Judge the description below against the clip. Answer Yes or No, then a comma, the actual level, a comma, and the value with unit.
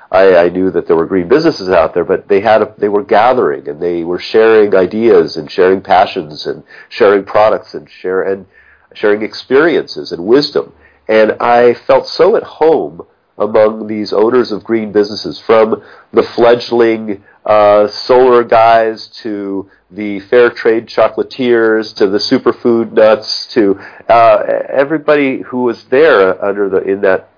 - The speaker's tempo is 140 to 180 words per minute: Yes, average, 155 wpm